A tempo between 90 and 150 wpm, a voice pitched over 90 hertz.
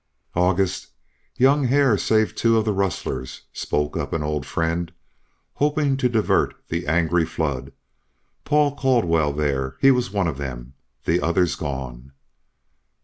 No: average, 140 wpm; very low, 85 Hz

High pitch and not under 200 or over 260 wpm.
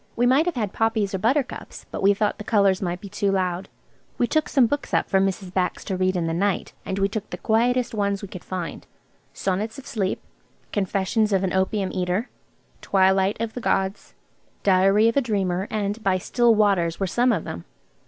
Yes: high, 200 Hz; fast, 205 wpm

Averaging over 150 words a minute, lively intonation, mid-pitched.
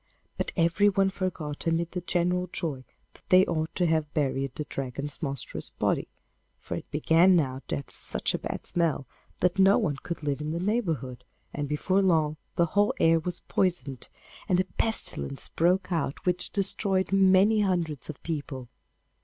No: average, 170 wpm; average, 4.1 semitones; medium, 170 Hz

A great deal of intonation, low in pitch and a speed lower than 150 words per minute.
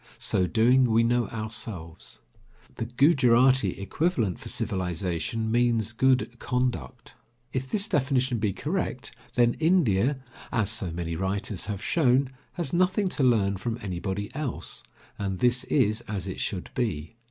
No: average, 4.8 semitones; low, 115 Hz; average, 140 wpm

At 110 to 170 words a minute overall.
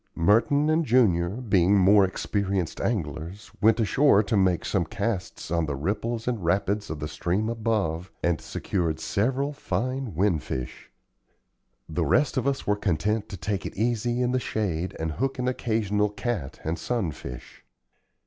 Yes: average, 160 wpm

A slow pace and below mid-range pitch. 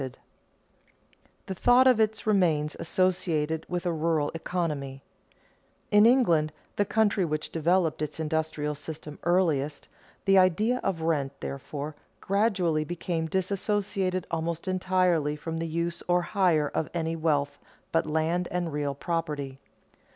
No: slow, 130 wpm; medium, 165 Hz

